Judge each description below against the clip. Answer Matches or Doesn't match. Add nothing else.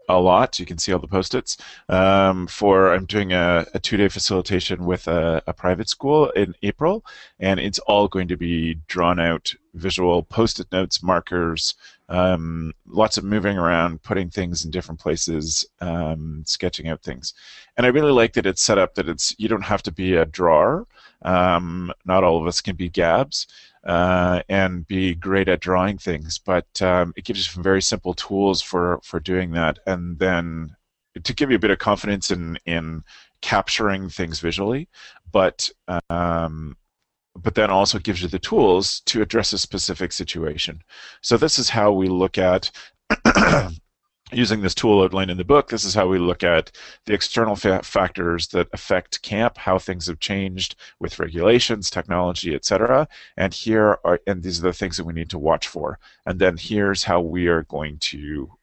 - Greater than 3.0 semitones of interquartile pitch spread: Doesn't match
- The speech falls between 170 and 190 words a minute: Matches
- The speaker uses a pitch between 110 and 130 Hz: Doesn't match